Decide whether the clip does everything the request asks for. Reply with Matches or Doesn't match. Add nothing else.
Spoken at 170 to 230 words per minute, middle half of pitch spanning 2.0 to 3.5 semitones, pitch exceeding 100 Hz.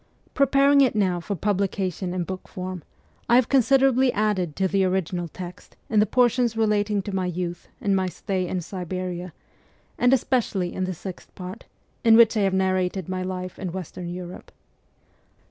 Matches